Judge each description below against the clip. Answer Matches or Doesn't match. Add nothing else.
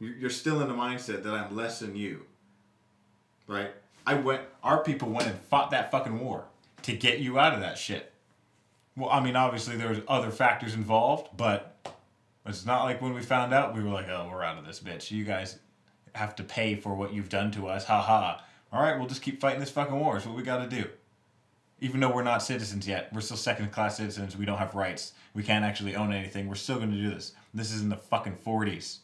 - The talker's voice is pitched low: Matches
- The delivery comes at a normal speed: Doesn't match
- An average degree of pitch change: Matches